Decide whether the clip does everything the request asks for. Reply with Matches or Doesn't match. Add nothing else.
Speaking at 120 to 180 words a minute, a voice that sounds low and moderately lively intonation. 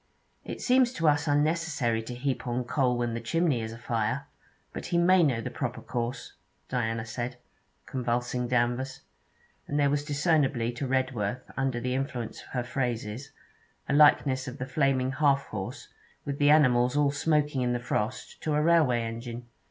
Matches